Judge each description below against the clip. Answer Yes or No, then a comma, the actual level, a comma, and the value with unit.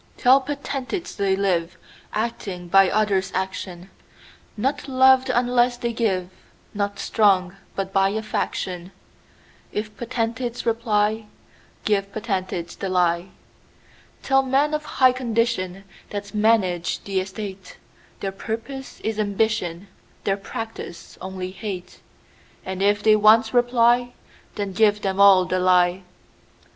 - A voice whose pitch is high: Yes, high, 205 Hz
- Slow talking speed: Yes, slow, 95 wpm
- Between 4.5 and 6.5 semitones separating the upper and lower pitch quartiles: No, average, 3.7 semitones